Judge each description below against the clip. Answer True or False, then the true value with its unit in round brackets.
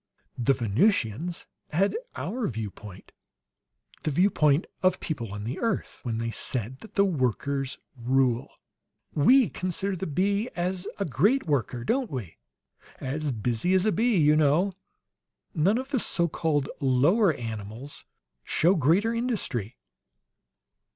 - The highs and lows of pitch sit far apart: True (7.8 semitones)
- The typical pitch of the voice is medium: True (150 Hz)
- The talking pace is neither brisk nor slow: False (130 wpm)